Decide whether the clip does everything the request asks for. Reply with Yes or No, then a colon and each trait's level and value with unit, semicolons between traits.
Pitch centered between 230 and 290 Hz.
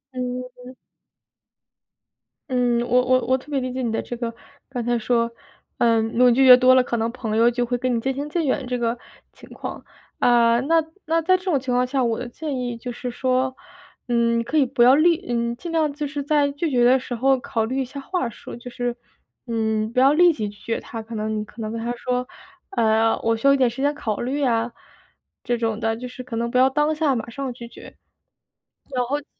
Yes: very high, 250 Hz